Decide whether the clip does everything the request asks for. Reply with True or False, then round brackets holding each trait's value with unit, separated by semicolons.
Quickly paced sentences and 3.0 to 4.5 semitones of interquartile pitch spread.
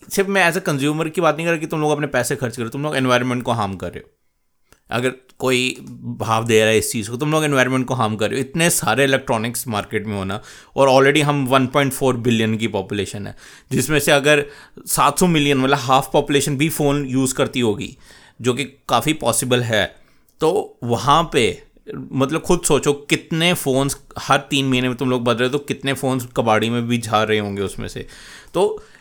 True (215 wpm; 3.7 semitones)